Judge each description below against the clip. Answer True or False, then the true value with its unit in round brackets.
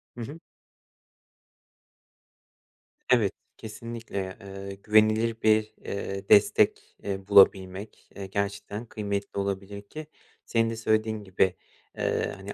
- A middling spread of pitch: False (2.1 semitones)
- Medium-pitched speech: False (100 Hz)